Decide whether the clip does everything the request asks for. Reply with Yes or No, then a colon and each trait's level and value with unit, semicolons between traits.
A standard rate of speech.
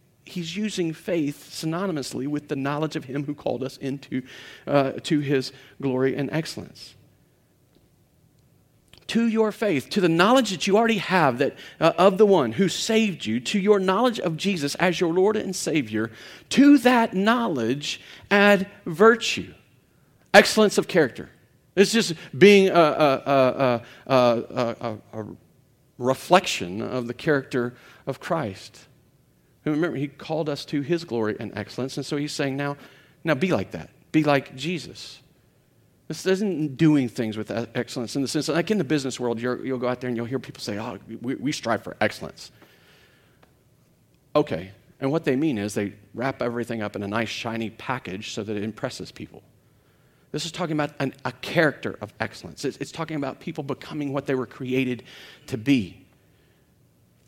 Yes: average, 170 wpm